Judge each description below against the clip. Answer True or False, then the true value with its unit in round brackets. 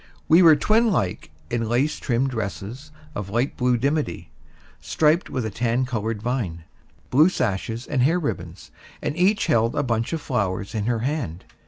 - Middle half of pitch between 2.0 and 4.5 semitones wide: False (5.3 semitones)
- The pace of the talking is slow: False (170 wpm)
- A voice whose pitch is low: True (120 Hz)